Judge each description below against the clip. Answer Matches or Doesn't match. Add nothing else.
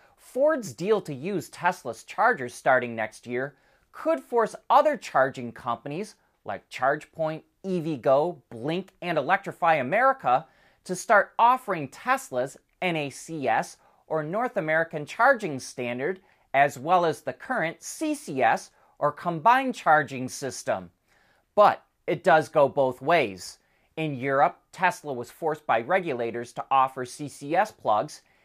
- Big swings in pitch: Matches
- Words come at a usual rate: Doesn't match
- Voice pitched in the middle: Matches